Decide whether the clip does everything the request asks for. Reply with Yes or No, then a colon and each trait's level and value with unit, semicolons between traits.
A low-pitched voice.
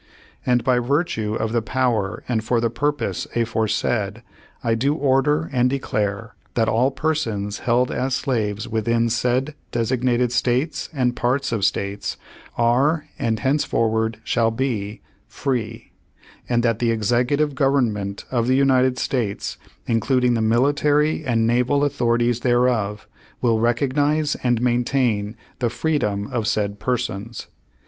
Yes: low, 120 Hz